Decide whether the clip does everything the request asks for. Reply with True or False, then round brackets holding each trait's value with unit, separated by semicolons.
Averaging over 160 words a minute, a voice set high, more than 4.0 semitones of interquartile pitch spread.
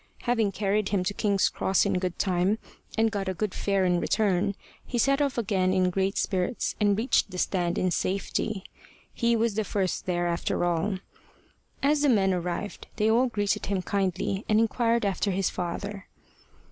False (180 wpm; 200 Hz; 2.9 semitones)